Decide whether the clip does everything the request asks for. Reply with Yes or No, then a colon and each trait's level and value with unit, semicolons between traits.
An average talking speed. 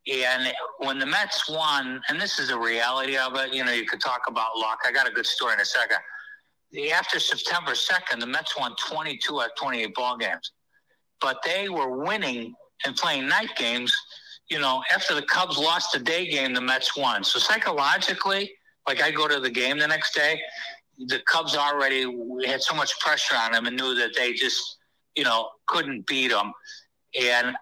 Yes: average, 195 wpm